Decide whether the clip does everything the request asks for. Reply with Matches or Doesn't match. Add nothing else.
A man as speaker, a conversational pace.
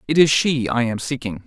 Doesn't match